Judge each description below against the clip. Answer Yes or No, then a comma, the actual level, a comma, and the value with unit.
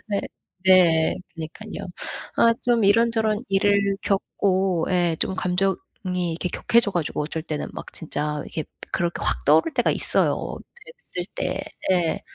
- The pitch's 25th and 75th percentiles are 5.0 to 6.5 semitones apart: No, average, 3.8 semitones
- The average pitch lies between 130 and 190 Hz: Yes, medium, 185 Hz